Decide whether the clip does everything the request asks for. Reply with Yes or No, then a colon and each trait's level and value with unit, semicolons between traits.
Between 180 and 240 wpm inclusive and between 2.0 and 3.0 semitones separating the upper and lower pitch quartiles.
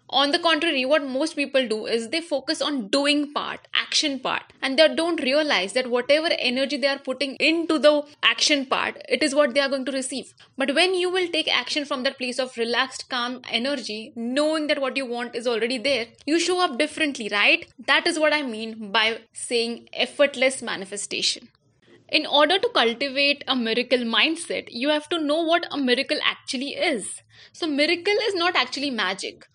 No: average, 190 wpm; average, 3.7 semitones